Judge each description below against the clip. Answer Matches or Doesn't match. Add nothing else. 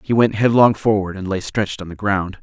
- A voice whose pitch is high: Doesn't match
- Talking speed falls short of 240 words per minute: Doesn't match